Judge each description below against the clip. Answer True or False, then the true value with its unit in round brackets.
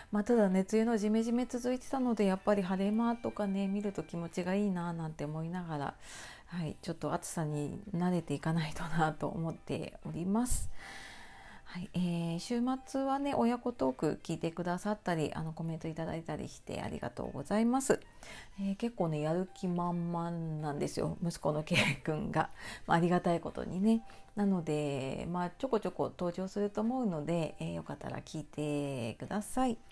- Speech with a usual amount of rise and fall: True (4.5 semitones)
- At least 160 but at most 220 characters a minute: False (375 characters per minute)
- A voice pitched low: False (175 Hz)